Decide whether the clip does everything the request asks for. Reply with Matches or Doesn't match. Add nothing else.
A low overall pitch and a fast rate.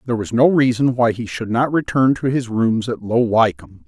Matches